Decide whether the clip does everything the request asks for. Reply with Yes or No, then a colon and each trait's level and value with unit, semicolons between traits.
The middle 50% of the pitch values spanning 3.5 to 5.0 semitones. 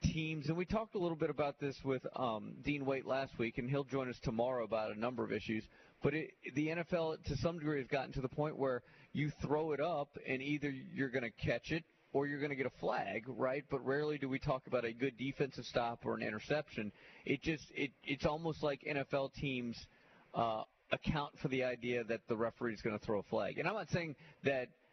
No: average, 3.0 semitones